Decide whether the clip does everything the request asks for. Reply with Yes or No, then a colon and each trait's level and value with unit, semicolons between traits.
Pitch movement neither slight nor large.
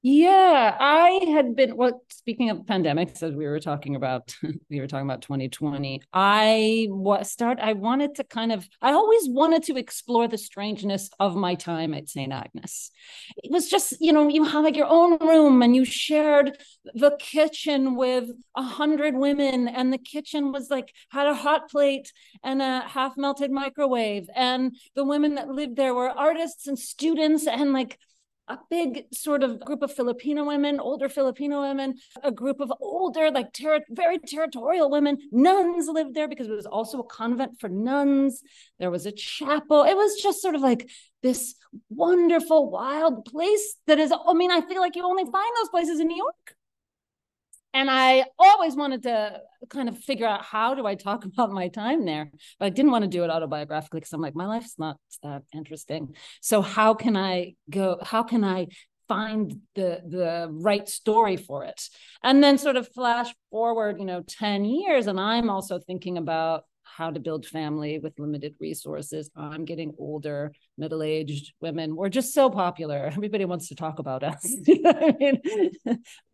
No: wide, 7.6 semitones